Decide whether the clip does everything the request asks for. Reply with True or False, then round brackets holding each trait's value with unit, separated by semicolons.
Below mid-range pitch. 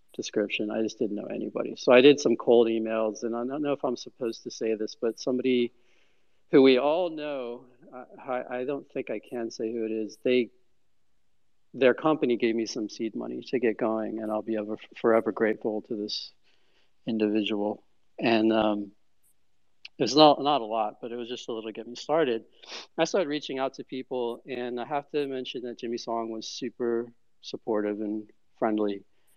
True (115 Hz)